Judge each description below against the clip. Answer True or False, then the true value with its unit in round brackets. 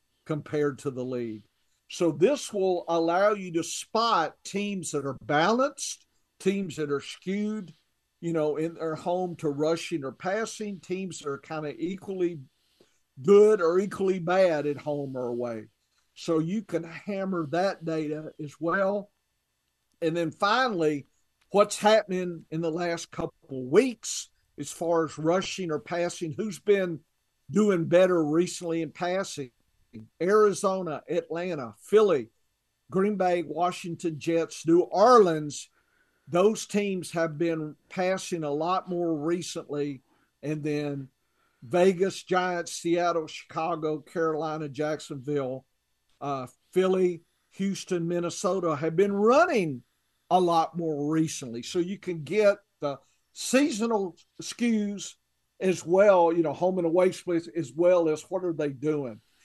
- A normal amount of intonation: True (3.7 semitones)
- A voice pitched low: False (170 Hz)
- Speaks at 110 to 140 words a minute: True (135 wpm)